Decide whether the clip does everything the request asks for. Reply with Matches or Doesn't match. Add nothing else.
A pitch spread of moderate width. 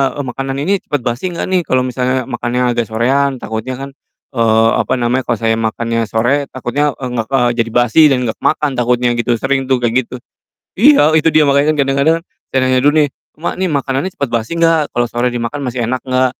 Matches